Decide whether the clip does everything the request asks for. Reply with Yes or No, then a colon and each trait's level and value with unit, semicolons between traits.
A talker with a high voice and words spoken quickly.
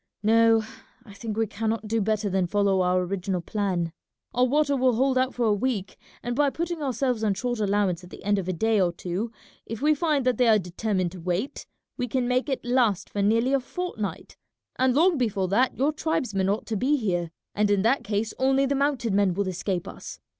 Yes: high, 220 Hz; fast, 220 wpm